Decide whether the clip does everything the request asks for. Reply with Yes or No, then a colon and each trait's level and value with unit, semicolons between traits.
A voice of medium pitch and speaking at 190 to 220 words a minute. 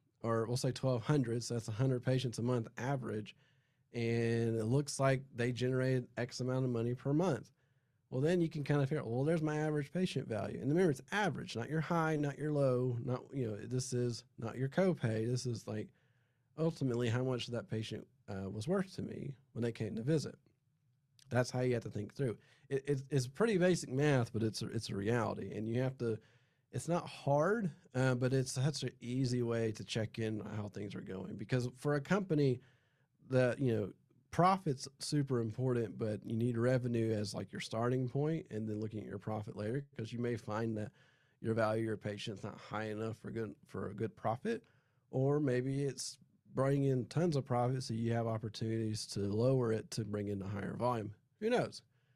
No: low, 125 Hz; fast, 205 wpm